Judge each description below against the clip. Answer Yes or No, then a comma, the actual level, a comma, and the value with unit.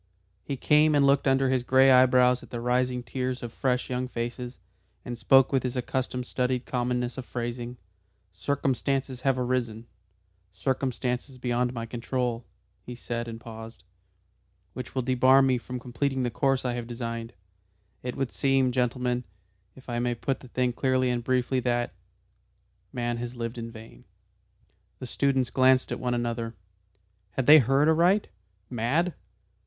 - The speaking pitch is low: Yes, low, 125 Hz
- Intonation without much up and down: Yes, narrow, 1.6 semitones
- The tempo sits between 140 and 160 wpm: Yes, average, 155 wpm